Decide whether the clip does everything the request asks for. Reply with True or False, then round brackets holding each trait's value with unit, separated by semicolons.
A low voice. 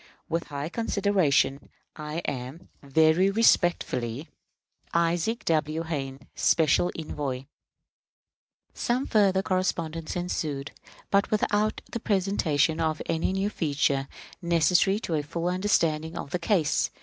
False (165 Hz)